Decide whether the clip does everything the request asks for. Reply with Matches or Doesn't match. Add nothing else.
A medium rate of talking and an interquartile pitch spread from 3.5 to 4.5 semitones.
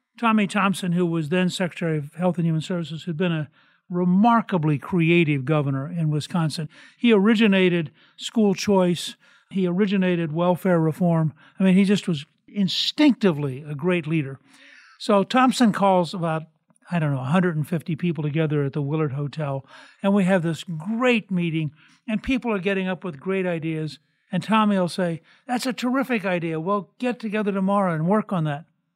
Matches